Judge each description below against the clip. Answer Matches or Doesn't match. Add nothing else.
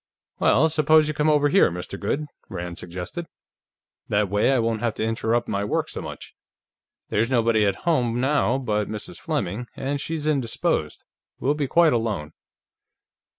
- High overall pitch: Doesn't match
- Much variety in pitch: Matches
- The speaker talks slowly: Doesn't match